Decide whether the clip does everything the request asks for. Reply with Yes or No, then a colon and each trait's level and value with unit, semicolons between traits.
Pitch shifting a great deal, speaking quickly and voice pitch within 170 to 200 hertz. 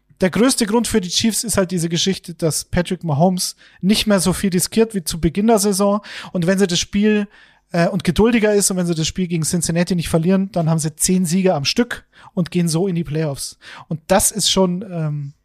No: average, 2.9 semitones; fast, 230 wpm; medium, 185 Hz